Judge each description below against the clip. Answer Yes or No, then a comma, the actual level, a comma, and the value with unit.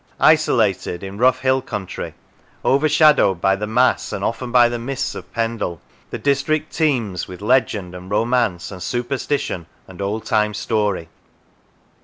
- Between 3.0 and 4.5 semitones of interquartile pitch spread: No, average, 5.0 semitones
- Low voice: Yes, low, 115 Hz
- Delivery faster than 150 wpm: No, average, 145 wpm